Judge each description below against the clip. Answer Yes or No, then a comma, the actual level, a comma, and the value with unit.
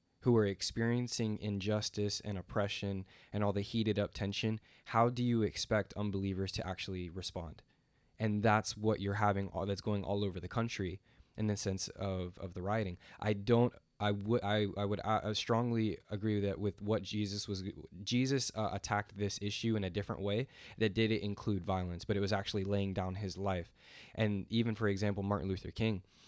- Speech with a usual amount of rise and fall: No, narrow, 2.0 semitones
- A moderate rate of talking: Yes, average, 185 wpm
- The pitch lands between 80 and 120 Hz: Yes, low, 105 Hz